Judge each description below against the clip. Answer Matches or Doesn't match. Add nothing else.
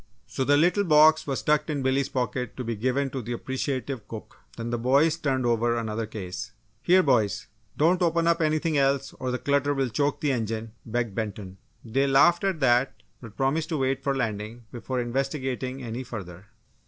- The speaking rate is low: Doesn't match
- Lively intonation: Doesn't match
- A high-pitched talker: Doesn't match